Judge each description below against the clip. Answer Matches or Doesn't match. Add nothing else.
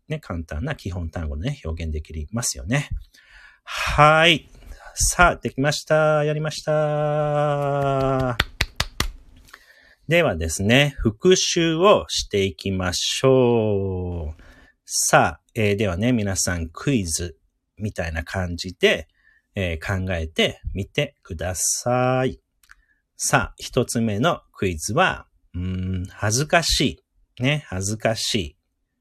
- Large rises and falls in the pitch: Matches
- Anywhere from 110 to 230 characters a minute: Matches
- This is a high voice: Doesn't match